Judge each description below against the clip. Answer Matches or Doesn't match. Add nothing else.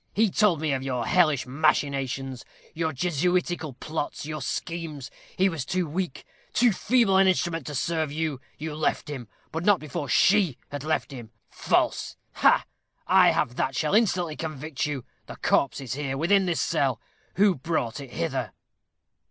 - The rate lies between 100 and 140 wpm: Doesn't match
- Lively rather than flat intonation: Doesn't match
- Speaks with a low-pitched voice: Doesn't match